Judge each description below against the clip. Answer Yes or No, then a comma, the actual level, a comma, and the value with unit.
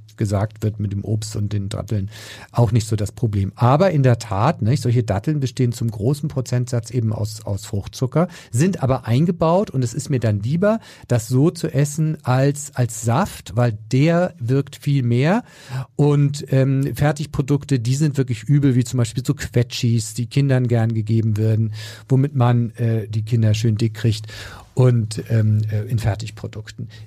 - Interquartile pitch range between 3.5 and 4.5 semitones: Yes, average, 3.9 semitones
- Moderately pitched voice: No, low, 120 Hz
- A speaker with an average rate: Yes, average, 175 wpm